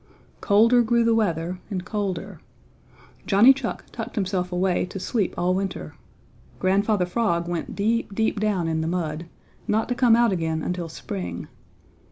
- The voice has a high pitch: Yes, high, 195 Hz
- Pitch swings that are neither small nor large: Yes, average, 4.2 semitones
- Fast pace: No, average, 155 wpm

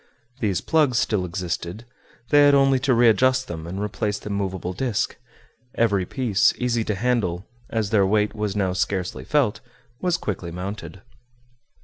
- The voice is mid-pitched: No, low, 105 Hz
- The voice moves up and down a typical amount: Yes, average, 4.6 semitones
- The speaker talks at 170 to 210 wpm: No, average, 150 wpm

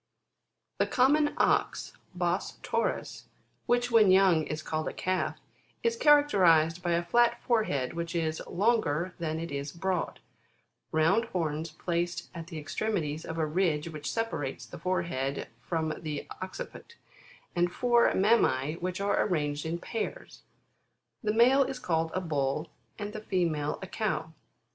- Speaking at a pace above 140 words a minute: Yes, average, 150 wpm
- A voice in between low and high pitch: Yes, medium, 170 Hz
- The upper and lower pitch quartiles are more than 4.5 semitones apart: Yes, average, 5.2 semitones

